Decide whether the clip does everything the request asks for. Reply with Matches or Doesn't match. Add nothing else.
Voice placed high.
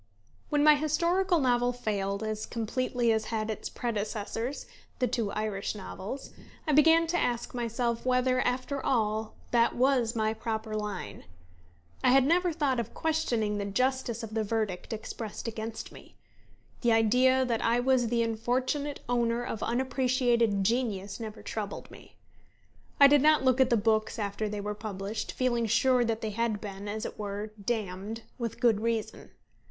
Matches